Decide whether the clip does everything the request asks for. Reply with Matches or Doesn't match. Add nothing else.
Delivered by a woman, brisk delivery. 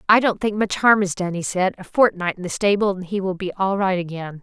Matches